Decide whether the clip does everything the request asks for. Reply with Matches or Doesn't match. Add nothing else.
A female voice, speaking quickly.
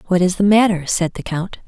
Matches